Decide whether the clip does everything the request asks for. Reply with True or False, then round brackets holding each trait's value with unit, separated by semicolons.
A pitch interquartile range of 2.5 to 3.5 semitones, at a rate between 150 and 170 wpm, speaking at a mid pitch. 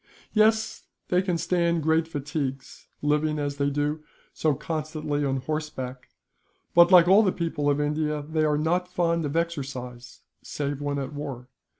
True (2.8 semitones; 160 wpm; 150 Hz)